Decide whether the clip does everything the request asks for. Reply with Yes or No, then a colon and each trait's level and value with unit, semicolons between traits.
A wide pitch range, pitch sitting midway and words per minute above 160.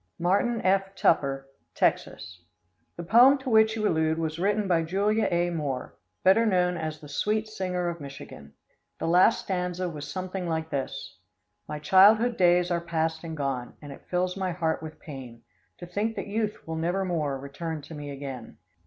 No: average, 4.1 semitones; medium, 175 Hz; average, 175 wpm